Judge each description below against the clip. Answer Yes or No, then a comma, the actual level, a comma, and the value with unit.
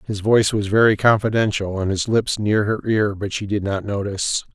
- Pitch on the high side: No, low, 105 Hz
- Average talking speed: No, fast, 210 wpm